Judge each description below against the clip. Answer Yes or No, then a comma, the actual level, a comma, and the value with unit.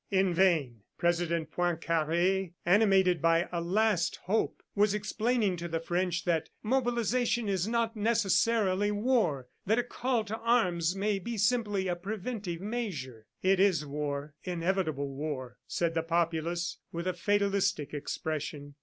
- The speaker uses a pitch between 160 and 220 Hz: Yes, medium, 185 Hz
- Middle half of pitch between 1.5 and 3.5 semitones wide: No, average, 4.2 semitones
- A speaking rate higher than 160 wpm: No, slow, 135 wpm